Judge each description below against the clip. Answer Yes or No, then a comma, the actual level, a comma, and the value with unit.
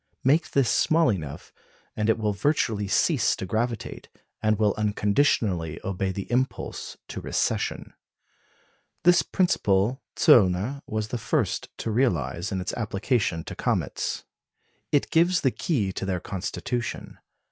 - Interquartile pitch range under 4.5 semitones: No, average, 5.1 semitones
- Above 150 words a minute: No, slow, 135 wpm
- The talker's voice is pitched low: Yes, low, 110 Hz